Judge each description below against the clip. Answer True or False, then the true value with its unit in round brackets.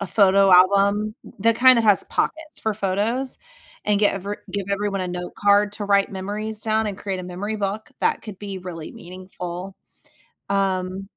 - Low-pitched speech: False (200 Hz)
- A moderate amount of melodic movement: False (2.0 semitones)